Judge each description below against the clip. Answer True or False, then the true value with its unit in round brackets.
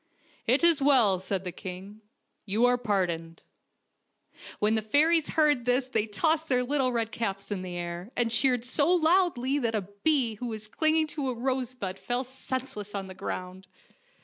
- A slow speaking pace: False (190 wpm)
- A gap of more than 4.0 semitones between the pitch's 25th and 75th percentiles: True (5.3 semitones)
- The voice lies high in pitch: True (240 Hz)